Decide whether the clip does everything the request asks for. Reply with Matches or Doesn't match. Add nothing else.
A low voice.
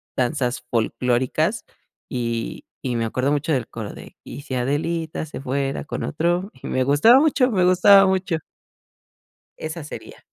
Doesn't match